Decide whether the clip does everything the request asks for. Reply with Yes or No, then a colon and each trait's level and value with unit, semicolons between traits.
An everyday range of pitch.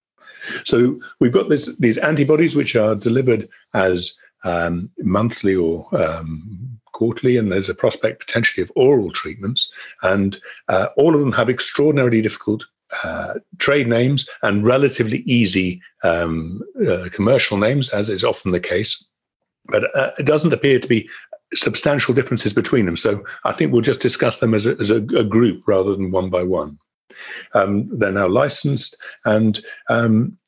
No: wide, 6.6 semitones